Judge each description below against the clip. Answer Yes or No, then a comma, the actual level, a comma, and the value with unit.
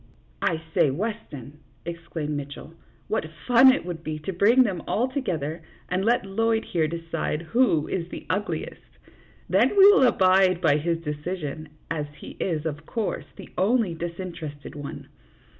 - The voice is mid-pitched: Yes, medium, 170 Hz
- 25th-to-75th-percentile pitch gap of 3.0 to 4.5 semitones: No, average, 5.2 semitones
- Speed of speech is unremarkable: Yes, average, 160 wpm